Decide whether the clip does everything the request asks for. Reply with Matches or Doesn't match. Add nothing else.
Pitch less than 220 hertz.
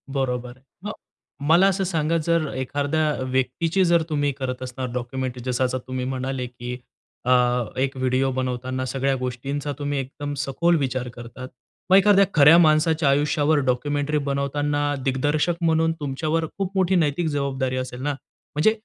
Matches